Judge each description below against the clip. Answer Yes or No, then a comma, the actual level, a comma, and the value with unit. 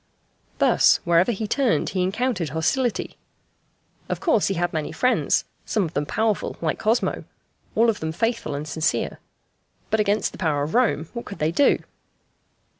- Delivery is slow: No, average, 165 wpm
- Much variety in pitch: Yes, wide, 6.2 semitones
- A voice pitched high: Yes, high, 195 Hz